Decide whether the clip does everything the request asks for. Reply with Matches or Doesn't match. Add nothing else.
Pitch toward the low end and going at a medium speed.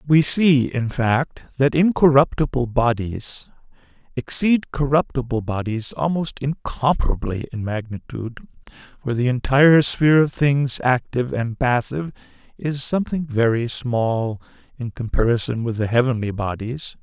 Doesn't match